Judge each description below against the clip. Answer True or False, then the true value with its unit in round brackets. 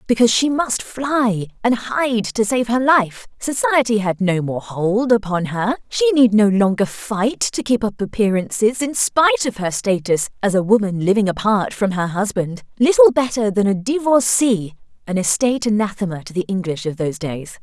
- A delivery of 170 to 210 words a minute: True (175 wpm)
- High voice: True (215 Hz)